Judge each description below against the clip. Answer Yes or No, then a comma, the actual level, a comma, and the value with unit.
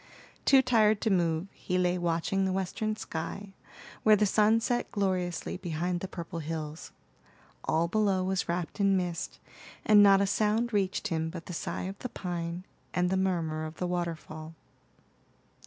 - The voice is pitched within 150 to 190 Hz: Yes, medium, 185 Hz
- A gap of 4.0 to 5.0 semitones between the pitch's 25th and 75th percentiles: No, average, 3.1 semitones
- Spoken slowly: No, average, 165 wpm